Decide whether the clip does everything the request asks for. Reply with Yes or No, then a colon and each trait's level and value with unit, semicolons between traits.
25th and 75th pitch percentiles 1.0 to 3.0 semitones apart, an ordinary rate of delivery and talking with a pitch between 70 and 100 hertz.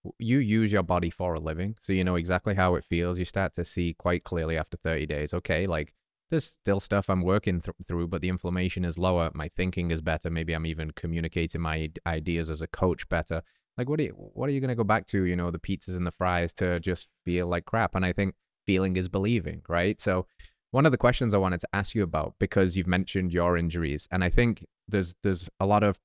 No: narrow, 2.6 semitones; fast, 245 wpm; very low, 90 Hz